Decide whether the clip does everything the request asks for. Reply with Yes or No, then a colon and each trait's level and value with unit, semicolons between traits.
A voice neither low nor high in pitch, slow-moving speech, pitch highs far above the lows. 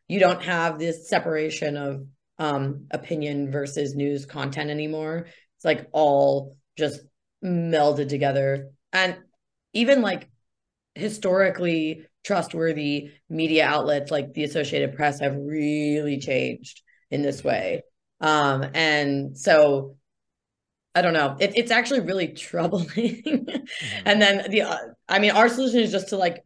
No: medium, 155 Hz; slow, 130 wpm; average, 4.6 semitones